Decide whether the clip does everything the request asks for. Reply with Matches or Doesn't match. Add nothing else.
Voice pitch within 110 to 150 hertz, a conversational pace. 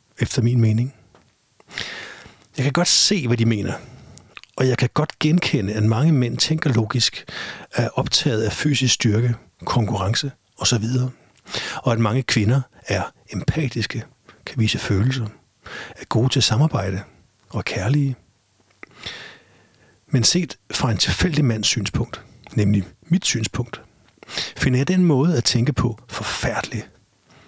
Doesn't match